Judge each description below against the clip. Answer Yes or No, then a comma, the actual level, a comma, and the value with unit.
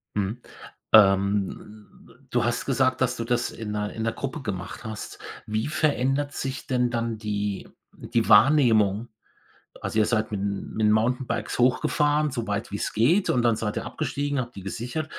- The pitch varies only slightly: No, average, 3.6 semitones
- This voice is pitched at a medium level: No, low, 115 Hz